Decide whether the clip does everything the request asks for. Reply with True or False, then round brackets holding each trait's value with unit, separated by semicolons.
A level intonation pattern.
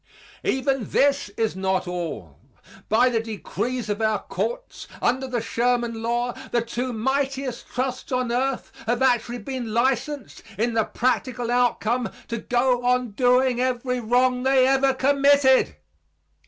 True (2.2 semitones)